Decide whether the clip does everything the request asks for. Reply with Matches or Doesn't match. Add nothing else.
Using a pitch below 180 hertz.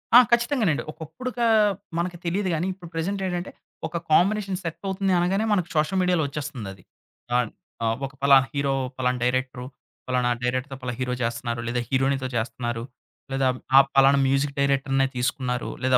Matches